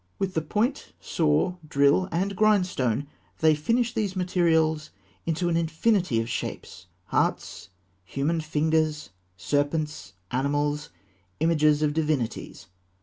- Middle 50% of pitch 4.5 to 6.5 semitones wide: No, average, 3.6 semitones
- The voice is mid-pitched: Yes, medium, 155 Hz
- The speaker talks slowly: Yes, slow, 110 wpm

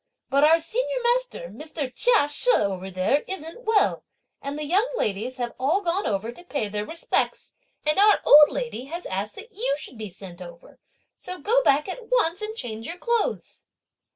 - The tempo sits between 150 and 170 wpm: No, average, 185 wpm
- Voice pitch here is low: No, very high, 305 Hz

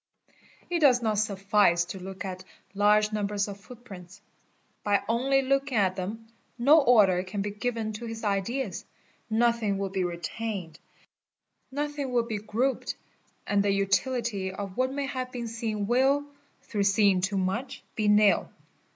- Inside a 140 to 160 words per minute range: Yes, average, 155 wpm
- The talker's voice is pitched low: No, high, 210 Hz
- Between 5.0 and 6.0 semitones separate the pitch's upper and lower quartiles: No, average, 3.7 semitones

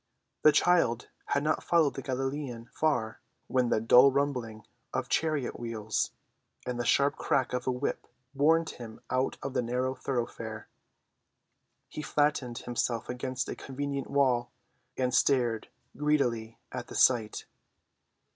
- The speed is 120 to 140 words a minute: Yes, slow, 135 wpm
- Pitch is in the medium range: No, low, 130 Hz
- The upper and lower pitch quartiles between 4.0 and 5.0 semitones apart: No, average, 3.0 semitones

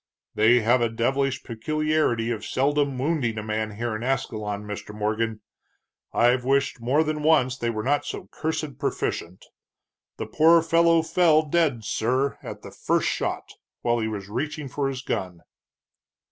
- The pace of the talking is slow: No, average, 160 wpm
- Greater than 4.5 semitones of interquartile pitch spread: Yes, average, 5.3 semitones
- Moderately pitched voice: No, low, 125 Hz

